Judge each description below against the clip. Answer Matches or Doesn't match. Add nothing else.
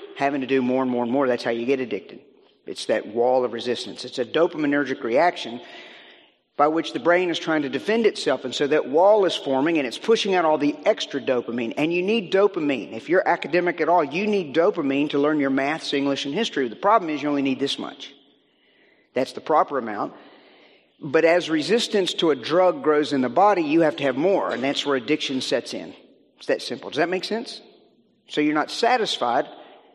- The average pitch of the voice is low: Doesn't match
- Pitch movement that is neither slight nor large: Matches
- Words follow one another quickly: Matches